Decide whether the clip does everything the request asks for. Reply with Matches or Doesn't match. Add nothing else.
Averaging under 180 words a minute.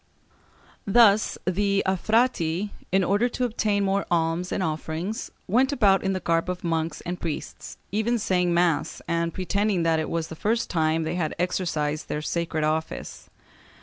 Matches